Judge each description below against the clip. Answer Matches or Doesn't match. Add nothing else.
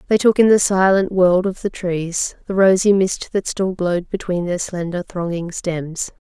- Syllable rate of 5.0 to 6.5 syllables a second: Doesn't match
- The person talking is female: Matches